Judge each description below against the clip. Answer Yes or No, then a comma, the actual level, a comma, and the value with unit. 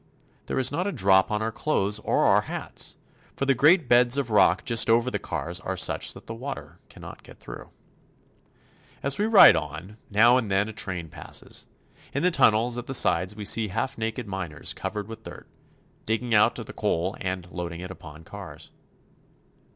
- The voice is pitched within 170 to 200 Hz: No, low, 110 Hz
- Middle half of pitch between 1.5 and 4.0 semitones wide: No, average, 4.7 semitones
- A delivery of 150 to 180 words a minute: No, average, 190 wpm